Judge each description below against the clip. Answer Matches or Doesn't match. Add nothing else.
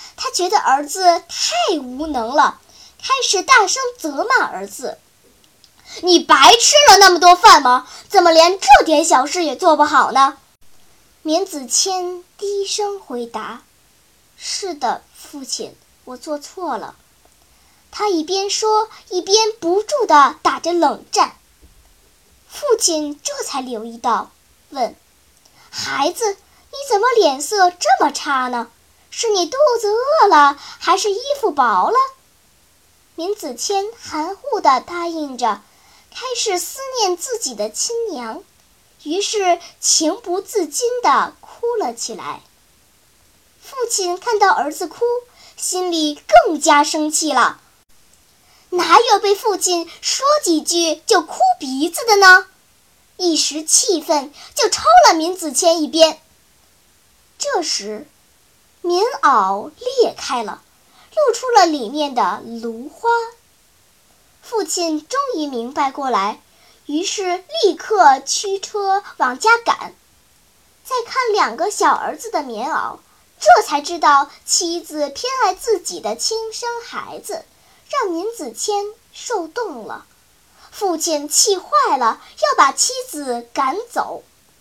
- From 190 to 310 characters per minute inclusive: Doesn't match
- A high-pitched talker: Matches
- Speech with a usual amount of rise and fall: Doesn't match